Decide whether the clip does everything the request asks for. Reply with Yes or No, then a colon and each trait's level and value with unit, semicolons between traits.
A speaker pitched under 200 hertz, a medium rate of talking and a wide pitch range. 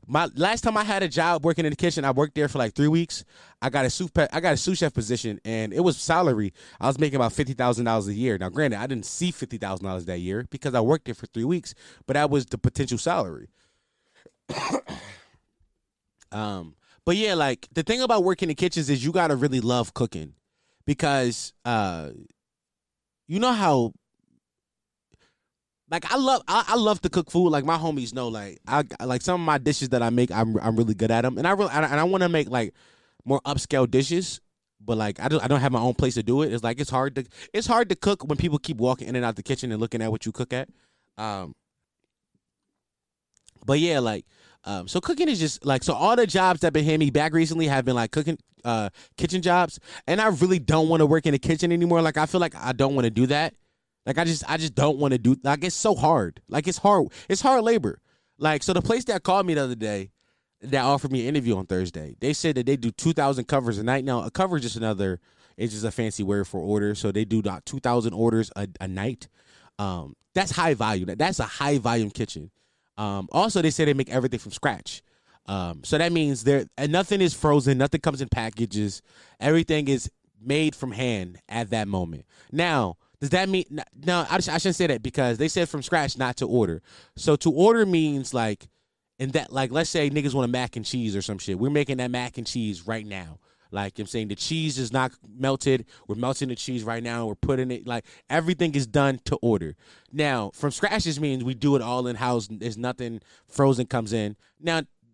No: low, 135 Hz; fast, 230 wpm; wide, 5.8 semitones